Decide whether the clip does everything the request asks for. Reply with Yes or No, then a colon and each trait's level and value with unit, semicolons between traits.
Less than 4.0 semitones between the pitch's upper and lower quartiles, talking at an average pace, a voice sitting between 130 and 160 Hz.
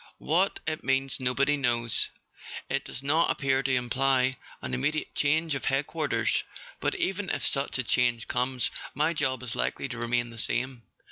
Yes: average, 3.0 semitones; average, 175 wpm; low, 135 Hz